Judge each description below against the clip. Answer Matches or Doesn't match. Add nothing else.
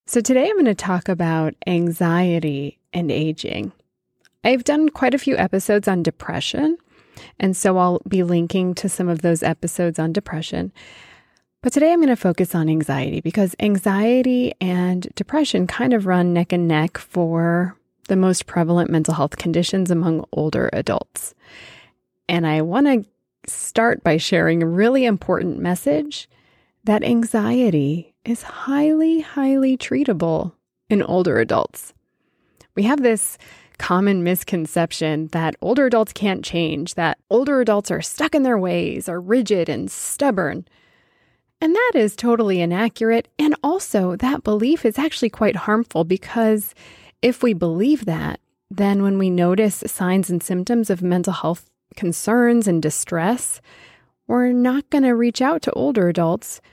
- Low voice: Doesn't match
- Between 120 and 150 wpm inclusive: Matches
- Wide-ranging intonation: Matches